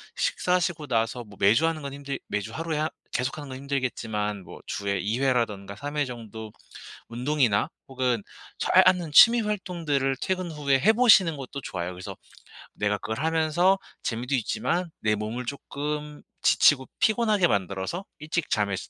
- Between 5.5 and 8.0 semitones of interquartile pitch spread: Yes, wide, 6.6 semitones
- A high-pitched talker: No, low, 135 Hz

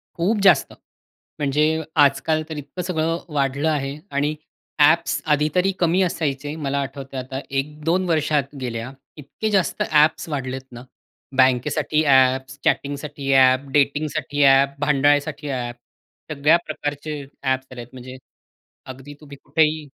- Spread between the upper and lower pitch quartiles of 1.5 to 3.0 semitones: Yes, narrow, 2.5 semitones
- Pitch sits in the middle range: Yes, medium, 145 Hz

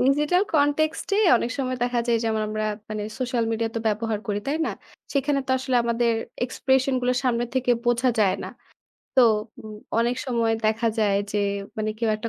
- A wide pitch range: No, average, 2.9 semitones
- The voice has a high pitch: Yes, high, 240 Hz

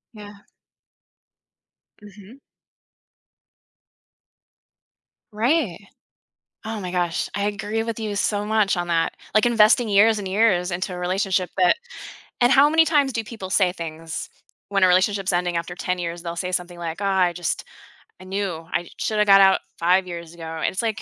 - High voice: Yes, high, 195 Hz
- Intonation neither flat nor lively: Yes, average, 3.2 semitones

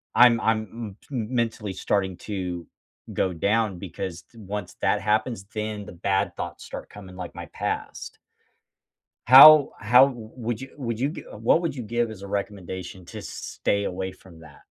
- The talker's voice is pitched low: Yes, low, 105 Hz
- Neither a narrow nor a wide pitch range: Yes, average, 3.7 semitones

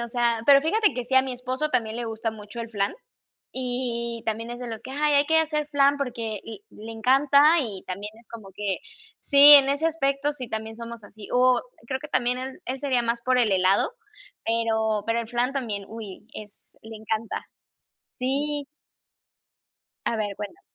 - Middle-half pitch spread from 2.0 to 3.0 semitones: No, average, 3.7 semitones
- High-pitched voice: Yes, high, 240 Hz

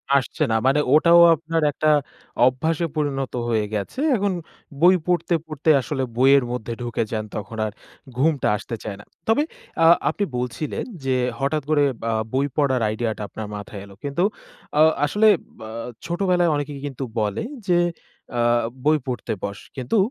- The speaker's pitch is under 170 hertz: Yes, medium, 140 Hz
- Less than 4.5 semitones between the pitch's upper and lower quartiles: No, wide, 5.6 semitones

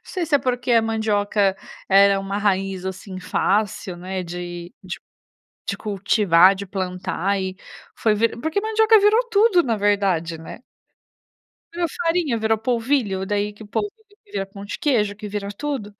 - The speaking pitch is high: Yes, high, 205 Hz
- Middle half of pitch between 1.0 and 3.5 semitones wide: No, average, 4.3 semitones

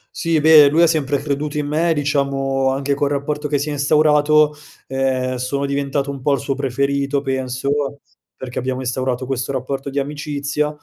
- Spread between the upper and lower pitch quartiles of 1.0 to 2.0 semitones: Yes, narrow, 1.7 semitones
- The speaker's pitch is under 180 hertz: Yes, medium, 140 Hz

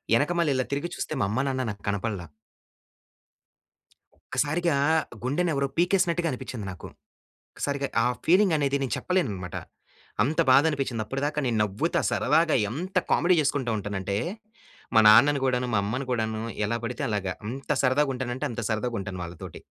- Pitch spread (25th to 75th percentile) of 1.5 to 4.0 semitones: No, average, 5.2 semitones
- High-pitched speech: No, low, 130 Hz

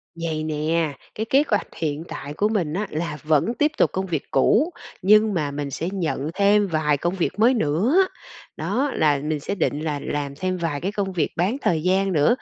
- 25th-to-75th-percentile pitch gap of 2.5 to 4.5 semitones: No, average, 5.1 semitones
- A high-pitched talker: No, medium, 170 Hz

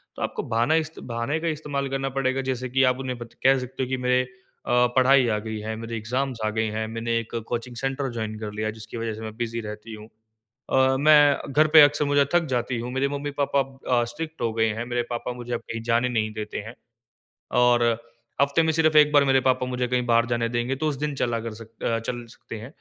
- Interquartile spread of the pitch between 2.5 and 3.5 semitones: Yes, average, 2.9 semitones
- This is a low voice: Yes, low, 125 Hz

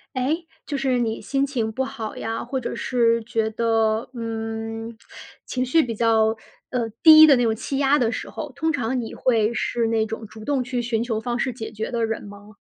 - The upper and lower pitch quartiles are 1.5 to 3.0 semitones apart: Yes, narrow, 2.5 semitones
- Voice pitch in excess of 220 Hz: Yes, high, 230 Hz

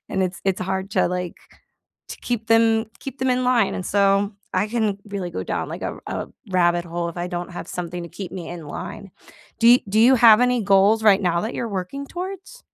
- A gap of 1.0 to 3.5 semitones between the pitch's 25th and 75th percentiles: No, average, 4.3 semitones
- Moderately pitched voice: No, high, 200 Hz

